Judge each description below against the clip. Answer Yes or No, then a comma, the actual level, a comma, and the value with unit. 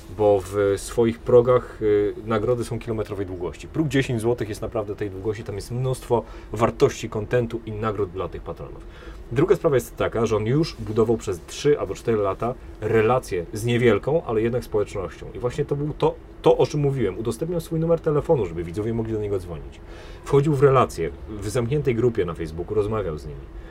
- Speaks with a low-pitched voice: Yes, low, 115 Hz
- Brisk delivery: Yes, fast, 185 wpm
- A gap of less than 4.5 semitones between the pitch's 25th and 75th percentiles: Yes, average, 3.9 semitones